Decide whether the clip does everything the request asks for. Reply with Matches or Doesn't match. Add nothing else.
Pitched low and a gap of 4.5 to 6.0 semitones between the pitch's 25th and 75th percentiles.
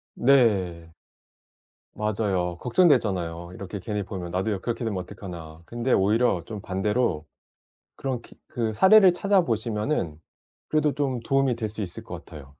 Matches